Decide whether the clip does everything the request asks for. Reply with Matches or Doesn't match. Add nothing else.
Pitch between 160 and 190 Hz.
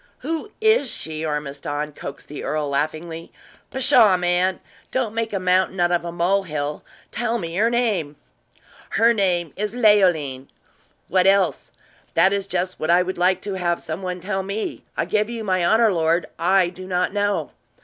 Matches